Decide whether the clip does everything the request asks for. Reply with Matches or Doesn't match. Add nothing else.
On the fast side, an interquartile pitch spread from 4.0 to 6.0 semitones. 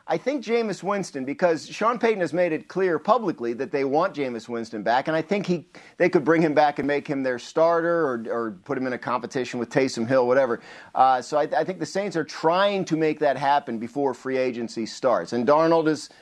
Matches